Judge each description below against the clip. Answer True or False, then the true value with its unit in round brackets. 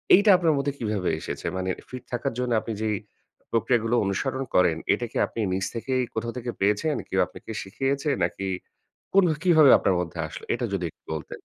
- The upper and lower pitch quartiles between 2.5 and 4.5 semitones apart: False (5.5 semitones)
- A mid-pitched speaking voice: False (115 Hz)